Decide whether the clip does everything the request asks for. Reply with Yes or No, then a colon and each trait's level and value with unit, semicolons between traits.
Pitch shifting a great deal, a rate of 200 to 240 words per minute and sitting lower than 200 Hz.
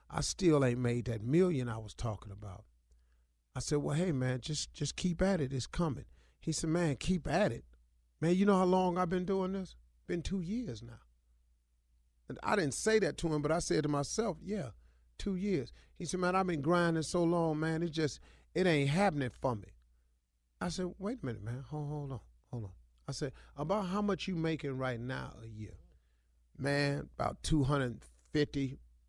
Yes: wide, 9.0 semitones; fast, 205 wpm; medium, 140 Hz